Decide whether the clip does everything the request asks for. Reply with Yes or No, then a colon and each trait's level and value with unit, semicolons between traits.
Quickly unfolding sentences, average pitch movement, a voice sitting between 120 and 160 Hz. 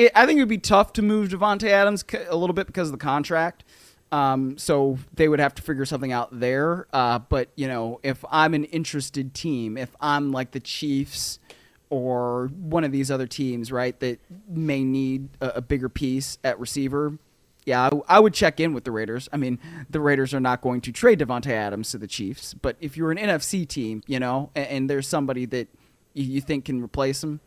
Yes: fast, 215 wpm; average, 3.8 semitones; medium, 140 Hz